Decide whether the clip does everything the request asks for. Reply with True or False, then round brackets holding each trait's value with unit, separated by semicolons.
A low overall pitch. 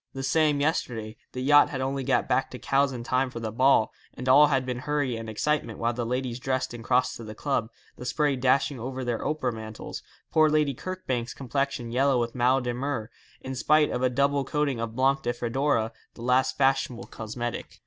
True (130 Hz)